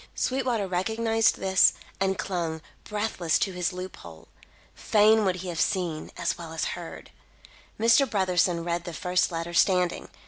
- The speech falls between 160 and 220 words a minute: No, average, 150 wpm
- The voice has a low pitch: No, medium, 180 Hz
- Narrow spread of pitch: No, average, 3.4 semitones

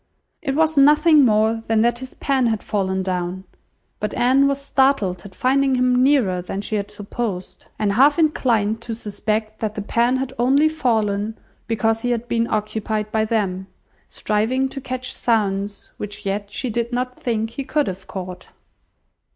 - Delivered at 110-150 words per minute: No, average, 170 wpm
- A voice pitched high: Yes, high, 225 Hz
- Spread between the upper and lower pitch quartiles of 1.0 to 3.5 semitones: No, average, 3.9 semitones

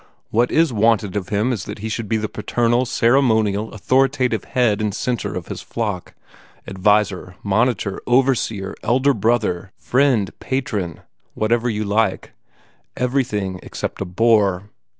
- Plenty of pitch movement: No, average, 3.3 semitones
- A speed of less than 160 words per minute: Yes, average, 140 wpm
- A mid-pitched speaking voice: No, low, 110 Hz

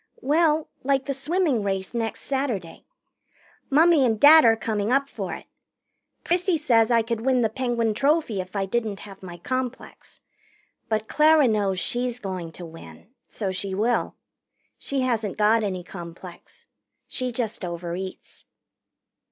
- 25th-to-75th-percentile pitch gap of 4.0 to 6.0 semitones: Yes, wide, 5.6 semitones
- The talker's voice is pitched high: Yes, high, 230 Hz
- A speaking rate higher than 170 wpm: No, average, 145 wpm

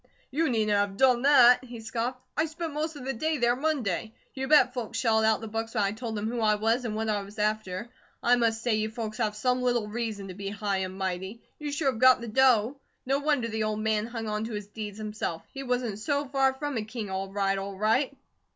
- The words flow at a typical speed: No, fast, 245 wpm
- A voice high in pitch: Yes, high, 225 Hz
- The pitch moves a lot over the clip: No, average, 3.2 semitones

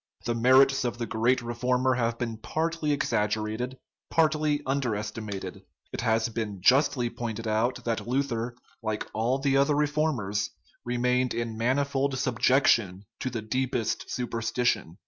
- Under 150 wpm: Yes, average, 140 wpm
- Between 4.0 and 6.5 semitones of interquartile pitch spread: No, average, 3.2 semitones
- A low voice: Yes, low, 120 Hz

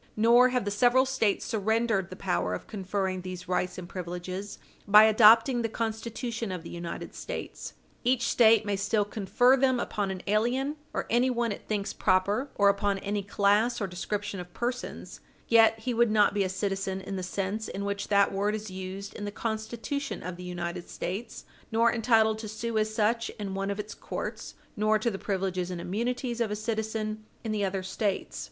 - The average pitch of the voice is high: Yes, high, 210 Hz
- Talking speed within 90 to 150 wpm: No, average, 190 wpm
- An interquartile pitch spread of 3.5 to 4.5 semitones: No, average, 3.0 semitones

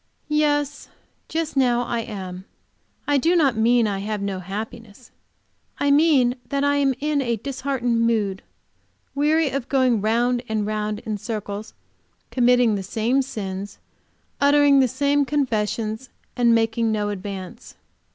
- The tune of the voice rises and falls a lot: No, average, 4.6 semitones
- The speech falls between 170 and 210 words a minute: No, average, 140 wpm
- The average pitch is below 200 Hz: No, high, 240 Hz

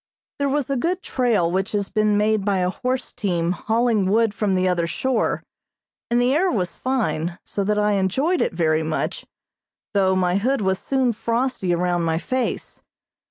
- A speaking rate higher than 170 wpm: Yes, average, 180 wpm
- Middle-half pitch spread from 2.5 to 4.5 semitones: No, wide, 5.4 semitones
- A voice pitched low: No, high, 210 Hz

